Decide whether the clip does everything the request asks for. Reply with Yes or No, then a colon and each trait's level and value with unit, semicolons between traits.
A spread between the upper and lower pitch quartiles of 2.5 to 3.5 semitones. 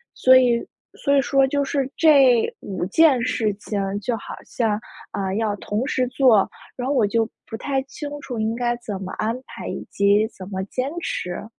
No: average, 4.2 semitones